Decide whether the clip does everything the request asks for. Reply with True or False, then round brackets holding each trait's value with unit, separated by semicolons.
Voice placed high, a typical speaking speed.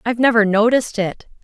True (225 Hz; 165 wpm)